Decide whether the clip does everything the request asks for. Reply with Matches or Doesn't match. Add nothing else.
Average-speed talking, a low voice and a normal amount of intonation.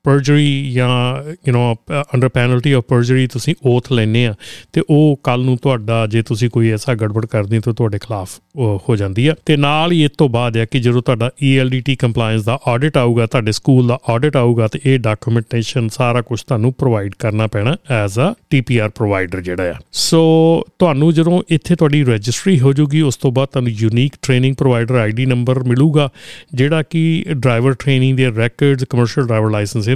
Doesn't match